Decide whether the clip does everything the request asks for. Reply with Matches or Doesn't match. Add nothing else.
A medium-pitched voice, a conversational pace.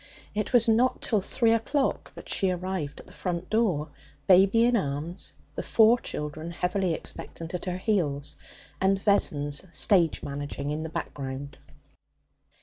Matches